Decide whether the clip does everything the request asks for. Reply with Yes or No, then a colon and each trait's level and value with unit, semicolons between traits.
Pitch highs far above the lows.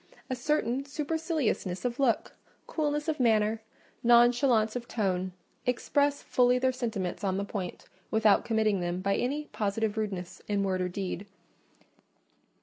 No: average, 4.5 semitones